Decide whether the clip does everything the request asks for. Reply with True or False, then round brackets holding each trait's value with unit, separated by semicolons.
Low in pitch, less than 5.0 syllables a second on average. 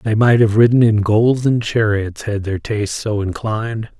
True (110 Hz; 4.6 syllables/s)